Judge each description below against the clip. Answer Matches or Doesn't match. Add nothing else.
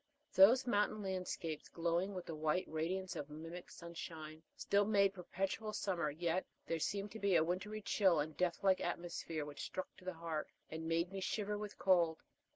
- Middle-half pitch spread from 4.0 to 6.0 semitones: Doesn't match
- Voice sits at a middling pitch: Matches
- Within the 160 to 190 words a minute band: Matches